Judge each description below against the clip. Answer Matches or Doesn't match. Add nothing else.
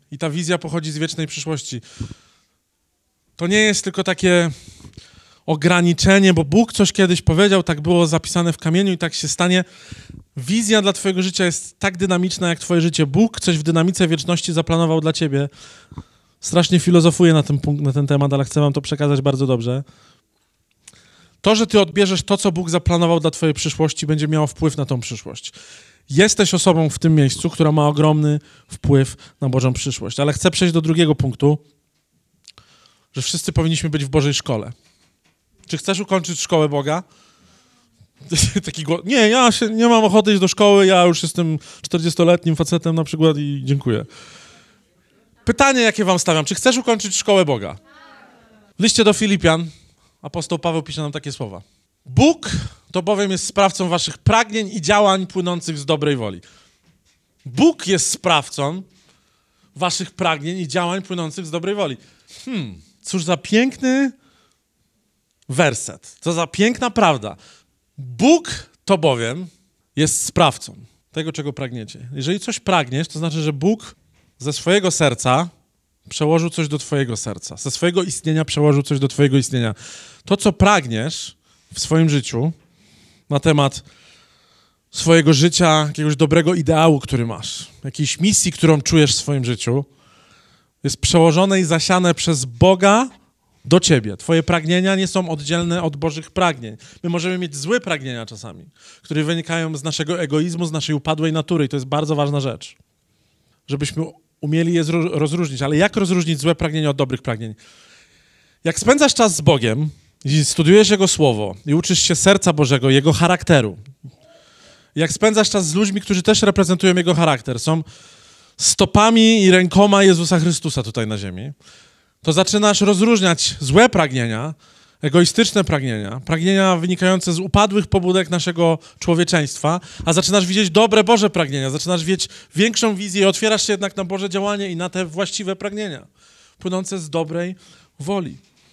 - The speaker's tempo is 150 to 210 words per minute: Matches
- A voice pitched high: Doesn't match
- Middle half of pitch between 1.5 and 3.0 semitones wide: Doesn't match